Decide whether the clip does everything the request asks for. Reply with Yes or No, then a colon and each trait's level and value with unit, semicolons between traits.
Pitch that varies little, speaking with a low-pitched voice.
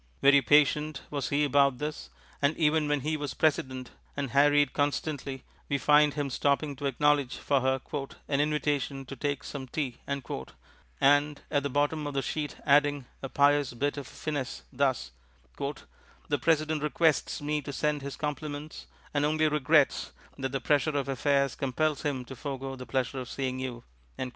No: narrow, 1.6 semitones; medium, 145 Hz